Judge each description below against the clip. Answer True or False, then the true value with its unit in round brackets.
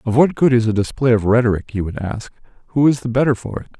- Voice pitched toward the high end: False (120 Hz)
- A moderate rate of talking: False (270 wpm)